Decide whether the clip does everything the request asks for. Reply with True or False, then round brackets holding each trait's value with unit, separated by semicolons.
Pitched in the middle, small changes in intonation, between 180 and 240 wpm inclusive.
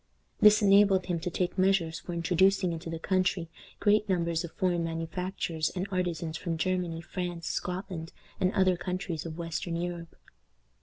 False (175 Hz; 2.1 semitones; 155 wpm)